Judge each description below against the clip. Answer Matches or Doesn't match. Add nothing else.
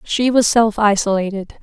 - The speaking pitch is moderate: Doesn't match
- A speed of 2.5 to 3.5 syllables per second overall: Doesn't match